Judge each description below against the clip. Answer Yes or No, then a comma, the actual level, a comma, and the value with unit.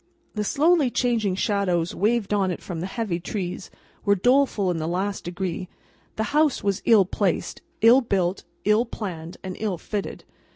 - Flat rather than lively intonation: No, average, 3.8 semitones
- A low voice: No, high, 200 Hz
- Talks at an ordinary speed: Yes, average, 165 wpm